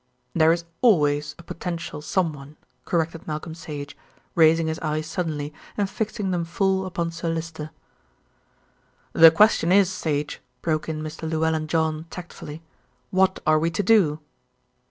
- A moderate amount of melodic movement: No, narrow, 2.2 semitones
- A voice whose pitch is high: No, medium, 165 Hz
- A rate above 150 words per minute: No, average, 140 wpm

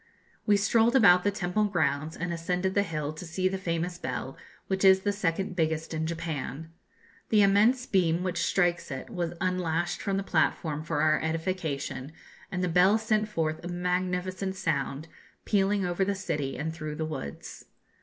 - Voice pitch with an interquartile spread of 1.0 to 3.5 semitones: Yes, average, 3.2 semitones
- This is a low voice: No, medium, 175 Hz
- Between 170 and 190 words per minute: Yes, average, 175 wpm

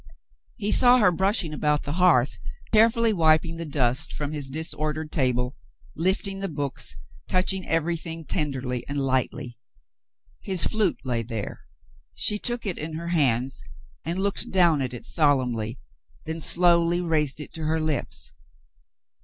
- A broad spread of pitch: No, average, 4.8 semitones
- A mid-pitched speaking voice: Yes, medium, 155 Hz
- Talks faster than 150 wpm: No, average, 145 wpm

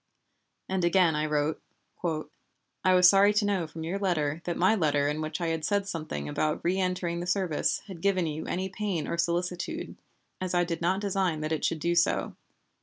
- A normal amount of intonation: Yes, average, 3.1 semitones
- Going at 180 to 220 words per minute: Yes, average, 195 wpm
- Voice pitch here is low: No, medium, 175 Hz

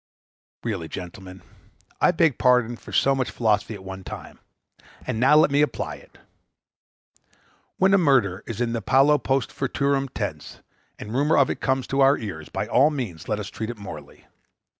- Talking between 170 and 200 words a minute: Yes, average, 185 wpm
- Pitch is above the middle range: No, low, 125 Hz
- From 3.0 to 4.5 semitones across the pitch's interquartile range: No, average, 5.2 semitones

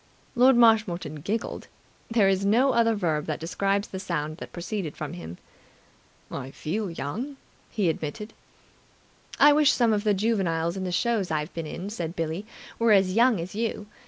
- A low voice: No, high, 195 Hz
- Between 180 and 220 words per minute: No, average, 170 wpm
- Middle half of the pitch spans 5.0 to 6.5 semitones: Yes, wide, 5.5 semitones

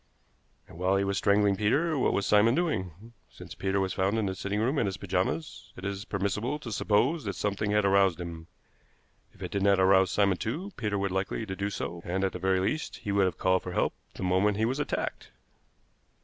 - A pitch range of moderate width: No, narrow, 2.1 semitones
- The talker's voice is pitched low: Yes, low, 100 Hz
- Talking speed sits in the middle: No, fast, 225 wpm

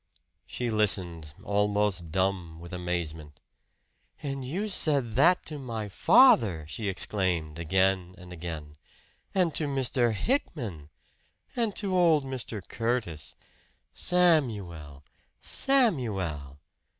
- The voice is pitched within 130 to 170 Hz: No, low, 105 Hz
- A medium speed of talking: No, slow, 100 wpm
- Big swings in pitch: Yes, wide, 8.2 semitones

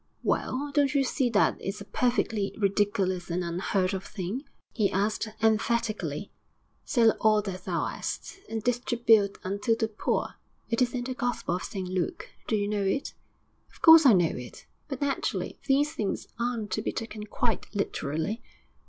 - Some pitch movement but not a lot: Yes, average, 3.8 semitones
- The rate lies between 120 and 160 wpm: No, average, 170 wpm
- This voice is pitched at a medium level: No, high, 215 Hz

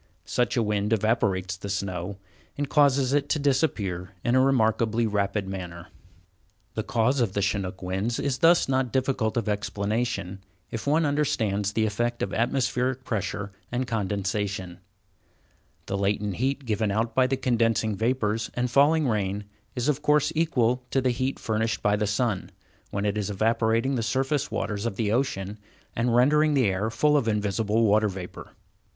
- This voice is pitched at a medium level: No, low, 115 Hz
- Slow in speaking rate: No, average, 165 wpm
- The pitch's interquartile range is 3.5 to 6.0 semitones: Yes, average, 4.2 semitones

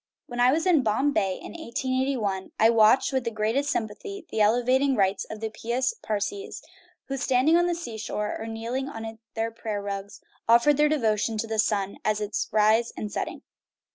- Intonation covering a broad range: No, average, 3.8 semitones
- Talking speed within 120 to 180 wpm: No, average, 195 wpm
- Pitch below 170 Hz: No, high, 225 Hz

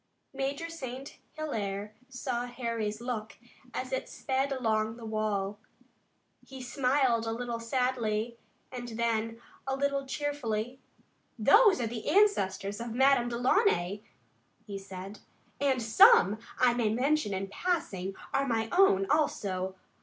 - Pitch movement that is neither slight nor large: Yes, average, 4.0 semitones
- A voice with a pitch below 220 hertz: No, high, 240 Hz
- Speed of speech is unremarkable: No, slow, 125 wpm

